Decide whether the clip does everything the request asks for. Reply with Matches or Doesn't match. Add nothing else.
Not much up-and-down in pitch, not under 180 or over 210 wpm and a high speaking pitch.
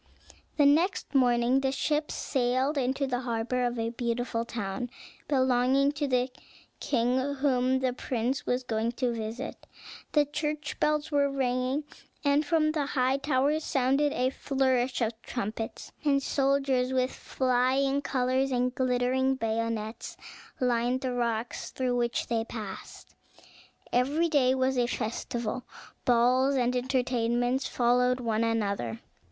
Doesn't match